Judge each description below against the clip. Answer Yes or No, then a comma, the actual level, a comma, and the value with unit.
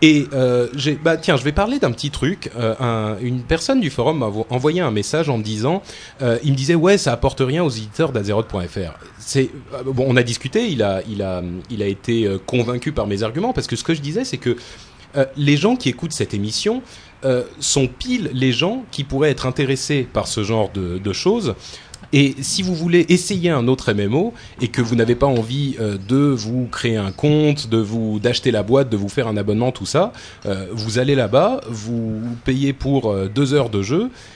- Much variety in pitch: No, average, 4.8 semitones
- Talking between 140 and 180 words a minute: No, average, 215 wpm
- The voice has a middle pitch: No, low, 130 Hz